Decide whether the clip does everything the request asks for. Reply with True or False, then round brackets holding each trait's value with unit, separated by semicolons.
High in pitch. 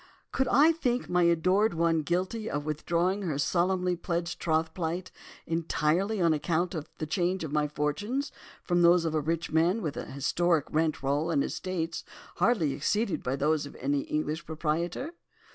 False (170 Hz)